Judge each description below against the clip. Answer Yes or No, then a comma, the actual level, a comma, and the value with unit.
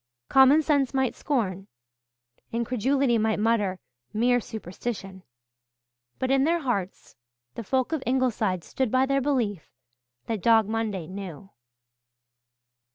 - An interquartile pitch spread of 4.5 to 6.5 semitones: Yes, average, 4.8 semitones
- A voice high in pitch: Yes, high, 230 Hz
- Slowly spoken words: Yes, slow, 115 wpm